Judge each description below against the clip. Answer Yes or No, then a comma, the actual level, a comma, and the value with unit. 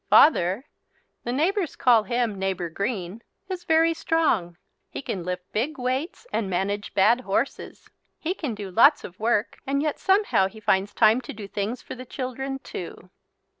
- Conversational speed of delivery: Yes, average, 170 wpm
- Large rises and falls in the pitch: Yes, wide, 6.1 semitones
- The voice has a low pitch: No, high, 235 Hz